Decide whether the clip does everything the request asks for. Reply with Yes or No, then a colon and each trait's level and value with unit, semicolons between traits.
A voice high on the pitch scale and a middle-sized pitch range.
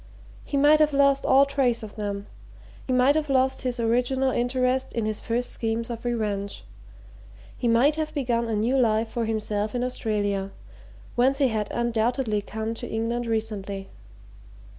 Yes: high, 235 Hz; average, 3.2 semitones